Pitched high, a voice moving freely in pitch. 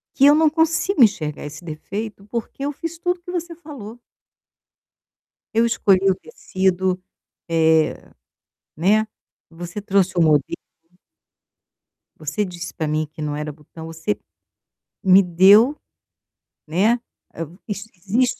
Yes: high, 195 Hz; wide, 6.7 semitones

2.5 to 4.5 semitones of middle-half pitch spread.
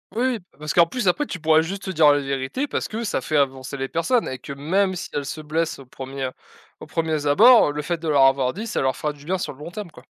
No: average, 5.2 semitones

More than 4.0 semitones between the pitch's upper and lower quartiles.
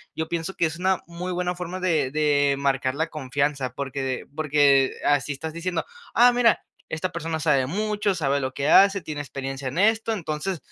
Yes: average, 4.5 semitones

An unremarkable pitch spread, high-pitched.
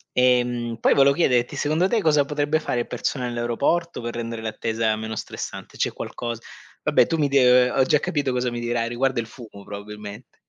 No: average, 3.2 semitones; low, 125 Hz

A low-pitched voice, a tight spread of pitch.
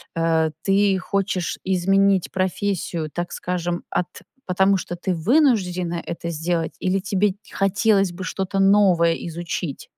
No: medium, 185 Hz; narrow, 2.3 semitones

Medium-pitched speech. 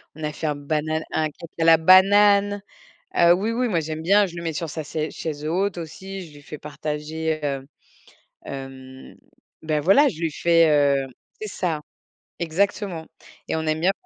Yes: medium, 160 Hz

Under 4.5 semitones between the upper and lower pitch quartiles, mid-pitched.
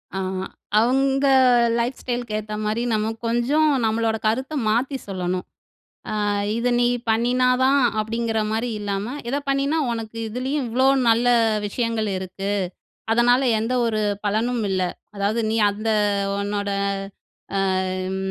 No: average, 2.9 semitones; high, 225 Hz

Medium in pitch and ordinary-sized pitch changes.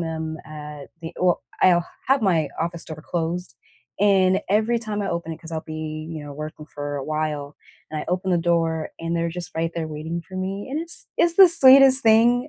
Yes: medium, 170 Hz; average, 4.2 semitones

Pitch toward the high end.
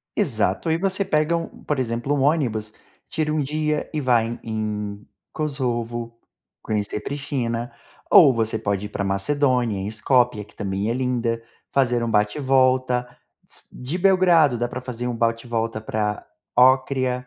No: low, 125 Hz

